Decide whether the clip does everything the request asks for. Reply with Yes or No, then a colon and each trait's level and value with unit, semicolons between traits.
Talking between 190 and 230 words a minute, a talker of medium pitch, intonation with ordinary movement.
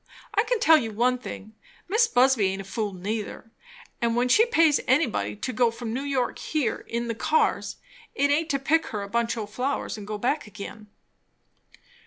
No: average, 195 wpm; high, 240 Hz; average, 4.8 semitones